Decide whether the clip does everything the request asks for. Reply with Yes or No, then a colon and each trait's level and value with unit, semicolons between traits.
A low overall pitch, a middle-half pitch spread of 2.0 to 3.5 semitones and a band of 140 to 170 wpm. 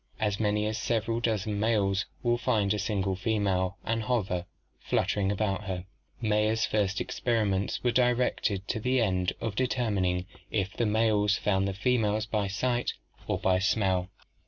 Yes: low, 105 Hz; narrow, 2.5 semitones; average, 155 wpm